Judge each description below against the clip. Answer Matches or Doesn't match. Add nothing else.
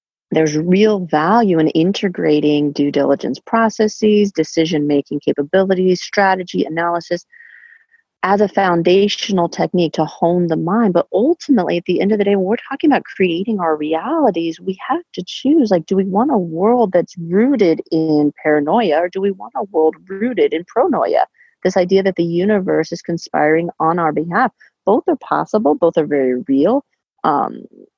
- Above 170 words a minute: Doesn't match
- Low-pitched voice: Doesn't match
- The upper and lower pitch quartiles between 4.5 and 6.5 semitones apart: Matches